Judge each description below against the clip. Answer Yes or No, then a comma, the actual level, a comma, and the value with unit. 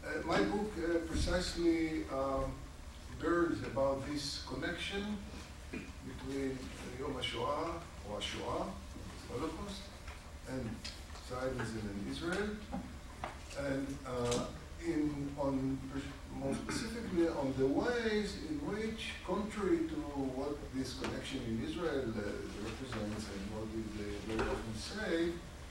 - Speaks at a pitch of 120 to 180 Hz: Yes, low, 135 Hz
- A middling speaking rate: No, slow, 105 wpm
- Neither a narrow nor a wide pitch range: No, wide, 7.5 semitones